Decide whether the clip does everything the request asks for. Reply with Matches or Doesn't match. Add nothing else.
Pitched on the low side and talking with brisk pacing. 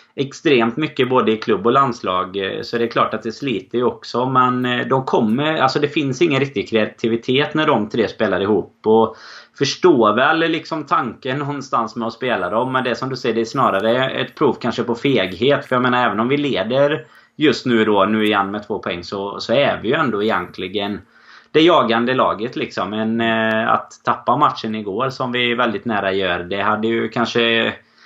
Matches